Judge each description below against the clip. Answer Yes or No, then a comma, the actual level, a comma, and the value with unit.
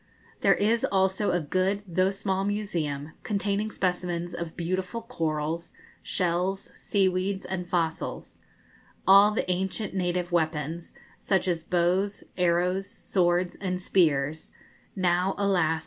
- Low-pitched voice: No, medium, 180 Hz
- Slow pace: Yes, slow, 115 wpm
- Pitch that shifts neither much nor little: No, narrow, 2.2 semitones